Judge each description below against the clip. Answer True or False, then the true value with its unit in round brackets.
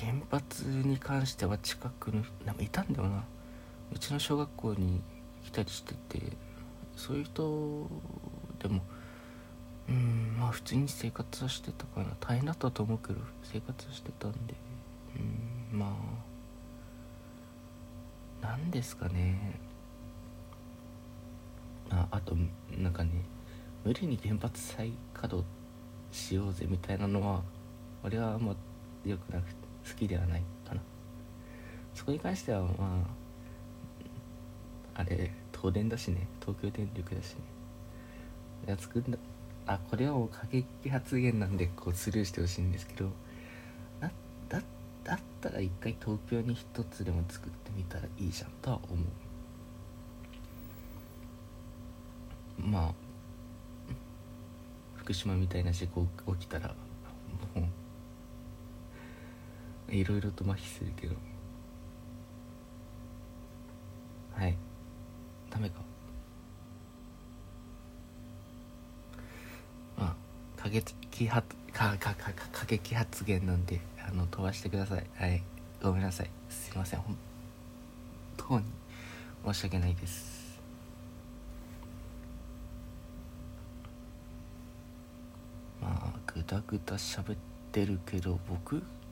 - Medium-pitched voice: False (100 Hz)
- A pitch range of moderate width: False (5.8 semitones)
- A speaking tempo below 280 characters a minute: True (200 characters per minute)